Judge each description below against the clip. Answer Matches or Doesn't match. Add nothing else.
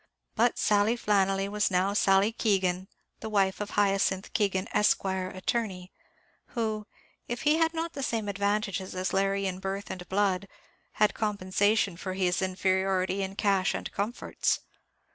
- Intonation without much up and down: Matches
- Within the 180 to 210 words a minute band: Doesn't match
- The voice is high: Matches